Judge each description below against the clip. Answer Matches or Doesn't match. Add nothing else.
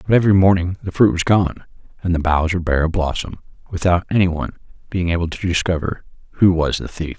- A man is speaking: Matches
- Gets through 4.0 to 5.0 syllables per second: Doesn't match